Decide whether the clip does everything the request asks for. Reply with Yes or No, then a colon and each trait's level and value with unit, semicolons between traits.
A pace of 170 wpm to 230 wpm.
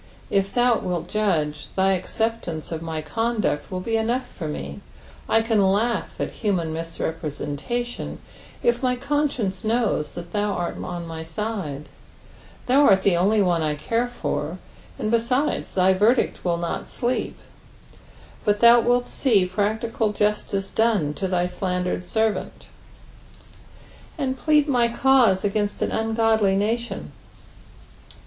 No: slow, 135 wpm